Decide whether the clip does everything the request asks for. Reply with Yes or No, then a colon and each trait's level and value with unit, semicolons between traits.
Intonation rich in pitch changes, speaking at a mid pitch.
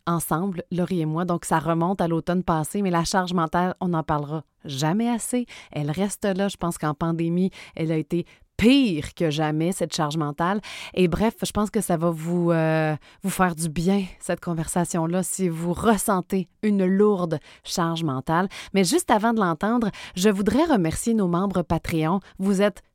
No: average, 3.2 semitones; medium, 175 Hz